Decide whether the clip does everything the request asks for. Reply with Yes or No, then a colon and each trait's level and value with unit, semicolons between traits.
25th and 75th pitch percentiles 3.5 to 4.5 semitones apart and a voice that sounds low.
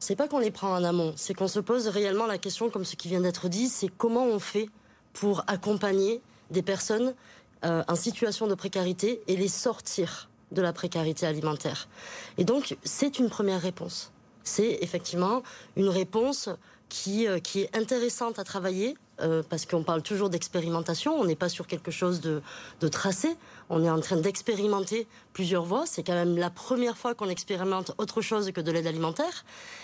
No: average, 4.2 semitones; high, 195 Hz